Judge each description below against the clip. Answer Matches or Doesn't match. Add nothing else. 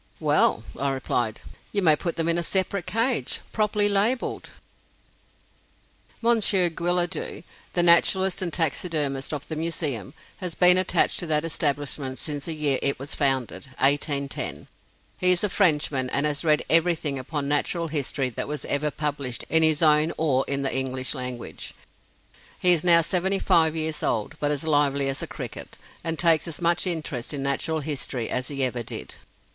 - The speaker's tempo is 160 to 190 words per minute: Matches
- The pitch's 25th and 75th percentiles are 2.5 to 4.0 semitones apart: Matches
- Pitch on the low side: Doesn't match